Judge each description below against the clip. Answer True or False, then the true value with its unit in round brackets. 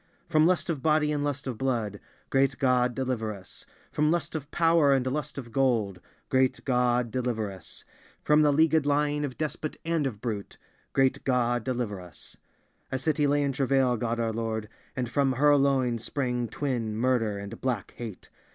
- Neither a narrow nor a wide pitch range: True (3.7 semitones)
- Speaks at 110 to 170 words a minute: True (160 wpm)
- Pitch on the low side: True (130 Hz)